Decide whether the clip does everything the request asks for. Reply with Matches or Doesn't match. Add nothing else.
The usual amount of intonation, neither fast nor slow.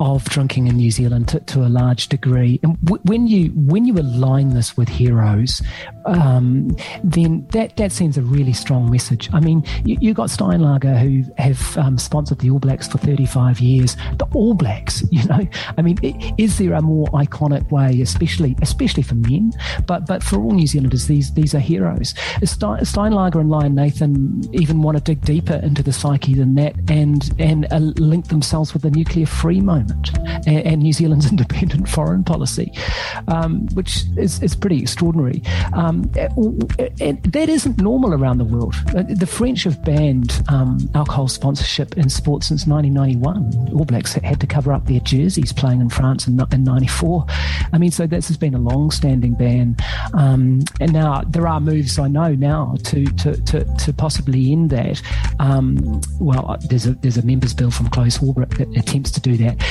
Matches